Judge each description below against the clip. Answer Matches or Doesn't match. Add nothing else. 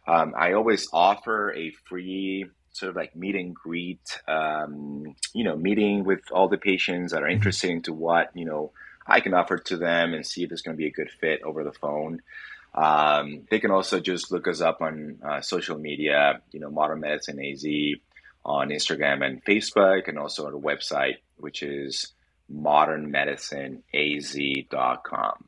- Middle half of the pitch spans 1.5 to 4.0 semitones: Matches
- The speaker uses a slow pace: Doesn't match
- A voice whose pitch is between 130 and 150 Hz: Doesn't match